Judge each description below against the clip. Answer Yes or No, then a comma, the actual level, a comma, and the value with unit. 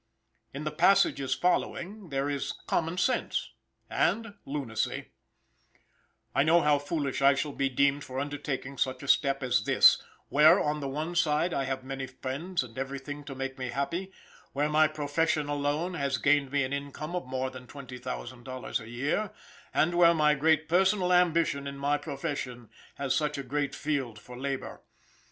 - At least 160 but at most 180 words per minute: Yes, average, 175 wpm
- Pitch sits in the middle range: Yes, medium, 145 Hz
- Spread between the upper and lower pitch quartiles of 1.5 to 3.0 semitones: Yes, average, 2.7 semitones